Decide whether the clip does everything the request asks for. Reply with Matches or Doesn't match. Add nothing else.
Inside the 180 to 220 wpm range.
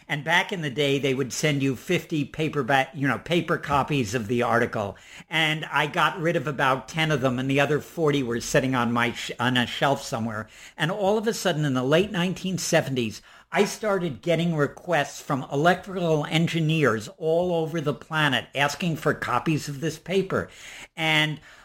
Matches